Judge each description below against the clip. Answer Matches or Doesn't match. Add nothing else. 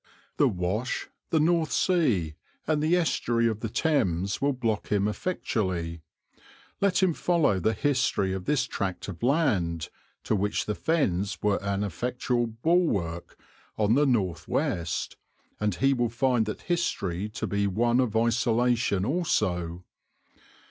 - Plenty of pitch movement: Matches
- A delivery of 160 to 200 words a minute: Doesn't match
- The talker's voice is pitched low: Matches